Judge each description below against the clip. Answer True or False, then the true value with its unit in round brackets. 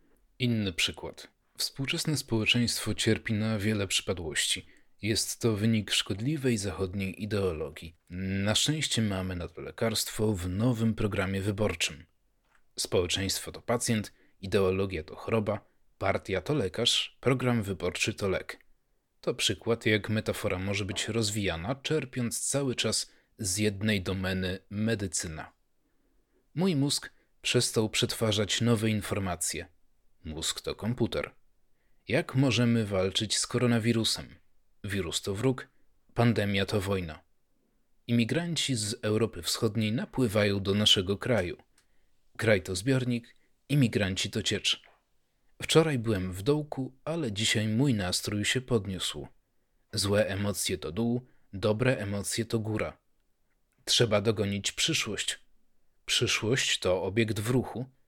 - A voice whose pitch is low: True (110 Hz)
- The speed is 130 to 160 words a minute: False (115 wpm)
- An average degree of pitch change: True (3.7 semitones)